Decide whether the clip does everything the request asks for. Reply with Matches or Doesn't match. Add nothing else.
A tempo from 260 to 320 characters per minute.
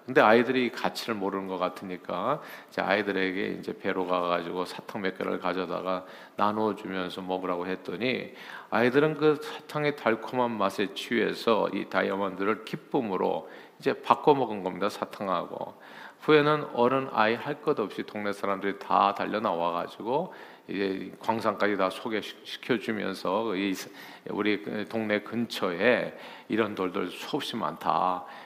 Matches